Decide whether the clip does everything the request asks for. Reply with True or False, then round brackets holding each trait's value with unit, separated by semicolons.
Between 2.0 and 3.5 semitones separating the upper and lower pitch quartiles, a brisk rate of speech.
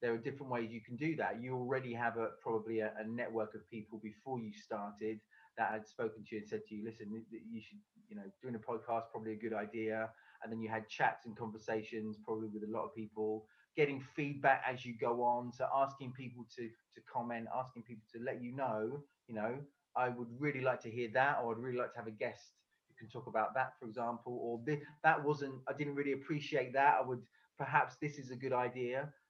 True (3.0 semitones; 230 wpm)